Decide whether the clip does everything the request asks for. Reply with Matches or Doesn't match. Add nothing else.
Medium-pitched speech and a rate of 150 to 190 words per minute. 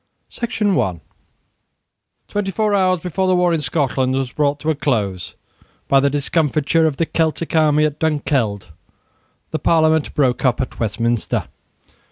Matches